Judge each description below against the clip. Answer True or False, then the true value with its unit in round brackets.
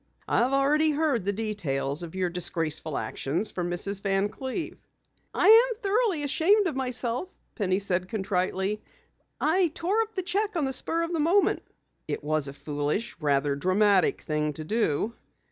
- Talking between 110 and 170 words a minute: True (160 wpm)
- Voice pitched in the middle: False (210 Hz)